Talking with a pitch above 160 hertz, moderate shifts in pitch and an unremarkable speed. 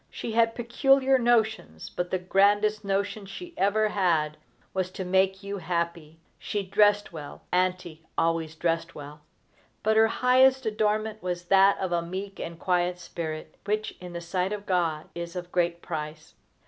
Yes: medium, 185 Hz; average, 3.8 semitones; average, 160 wpm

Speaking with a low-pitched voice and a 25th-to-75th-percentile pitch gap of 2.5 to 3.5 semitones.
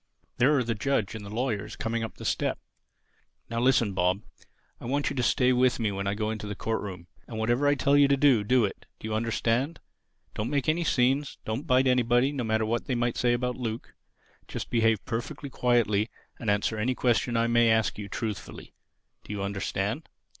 Yes: low, 115 Hz; average, 2.9 semitones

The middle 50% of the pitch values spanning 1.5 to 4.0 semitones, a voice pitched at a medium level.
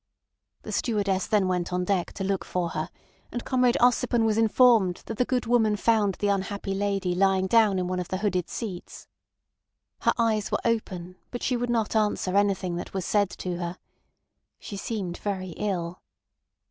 No: average, 3.4 semitones; high, 200 Hz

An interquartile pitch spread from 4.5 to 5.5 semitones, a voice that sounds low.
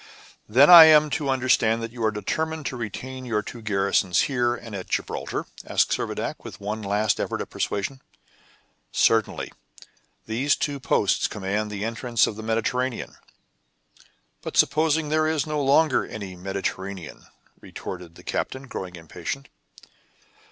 Yes: average, 5.2 semitones; low, 115 Hz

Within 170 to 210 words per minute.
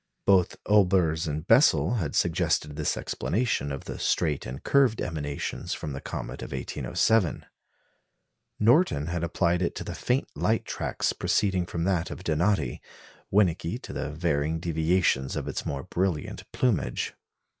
No: average, 145 wpm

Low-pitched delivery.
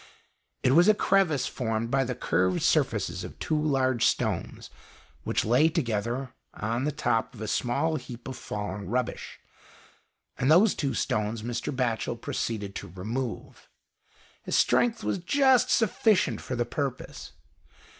Yes: low, 125 Hz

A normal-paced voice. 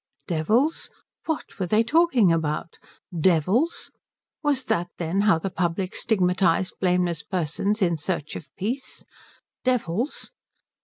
No: slow, 115 wpm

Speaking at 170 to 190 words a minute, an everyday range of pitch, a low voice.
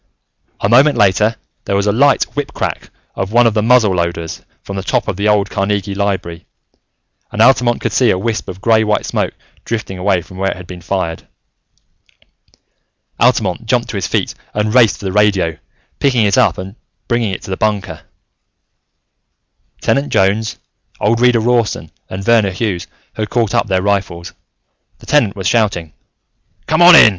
Yes: average, 175 wpm; average, 3.3 semitones; low, 105 Hz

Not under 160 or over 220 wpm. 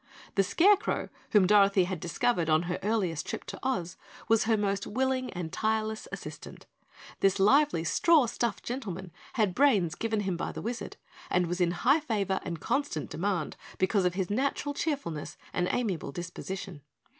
Yes: average, 165 wpm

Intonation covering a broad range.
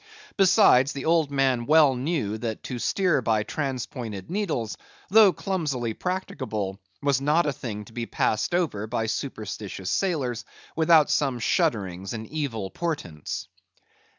Yes: wide, 6.3 semitones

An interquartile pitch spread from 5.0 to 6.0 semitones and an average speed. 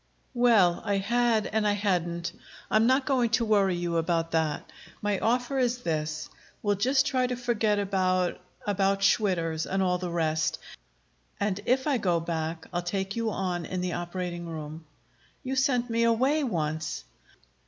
Yes: wide, 5.4 semitones; average, 165 wpm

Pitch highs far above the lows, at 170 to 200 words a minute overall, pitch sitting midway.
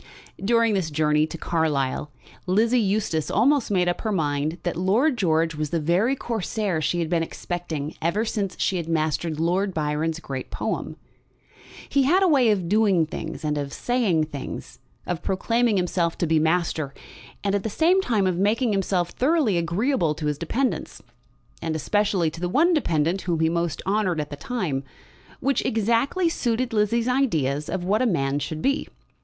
Yes: wide, 5.9 semitones; average, 175 wpm; medium, 180 Hz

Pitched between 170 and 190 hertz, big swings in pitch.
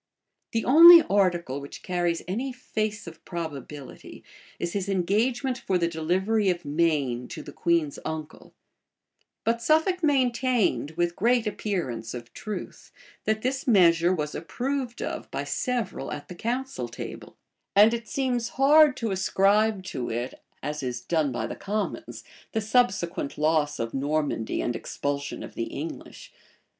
Yes: medium, 185 Hz; wide, 7.5 semitones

